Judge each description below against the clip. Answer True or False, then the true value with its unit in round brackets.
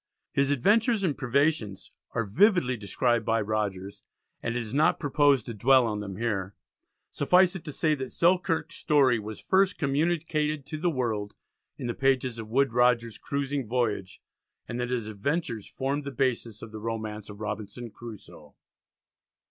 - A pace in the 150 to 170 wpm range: True (165 wpm)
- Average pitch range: True (5.0 semitones)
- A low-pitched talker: True (125 Hz)